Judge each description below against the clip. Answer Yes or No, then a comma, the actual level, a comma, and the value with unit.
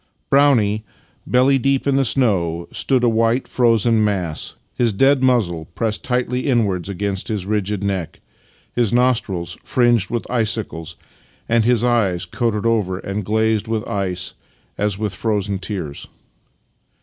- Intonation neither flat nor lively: Yes, average, 3.8 semitones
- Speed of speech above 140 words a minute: No, slow, 135 wpm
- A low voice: Yes, low, 110 Hz